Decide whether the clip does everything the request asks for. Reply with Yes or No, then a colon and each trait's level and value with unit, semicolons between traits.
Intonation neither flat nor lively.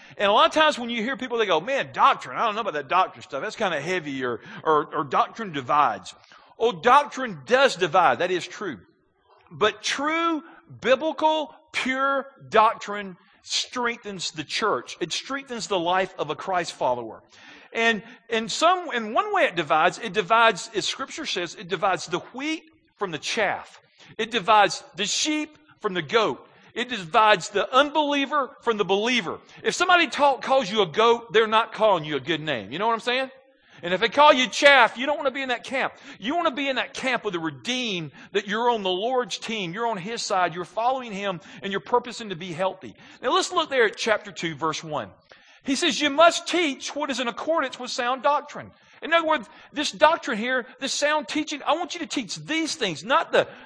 No: wide, 6.3 semitones